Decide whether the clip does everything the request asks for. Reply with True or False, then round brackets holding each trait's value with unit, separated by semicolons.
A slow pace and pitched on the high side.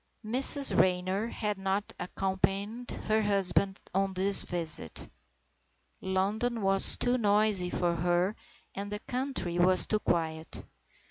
True (125 wpm; 195 Hz)